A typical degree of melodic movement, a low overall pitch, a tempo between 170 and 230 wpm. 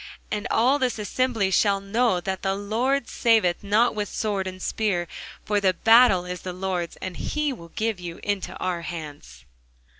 No: average, 3.8 semitones; high, 200 Hz; average, 175 wpm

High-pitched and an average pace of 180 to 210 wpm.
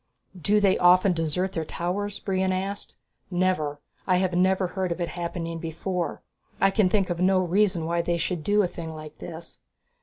No: medium, 180 Hz; average, 185 wpm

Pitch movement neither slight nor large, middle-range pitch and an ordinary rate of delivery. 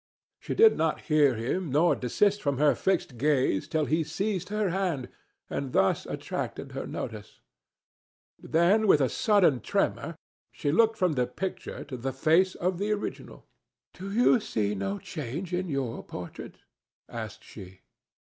No: wide, 6.6 semitones; medium, 160 Hz; average, 155 wpm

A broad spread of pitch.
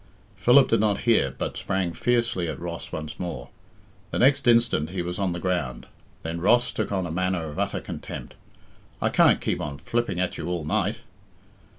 Yes: wide, 5.8 semitones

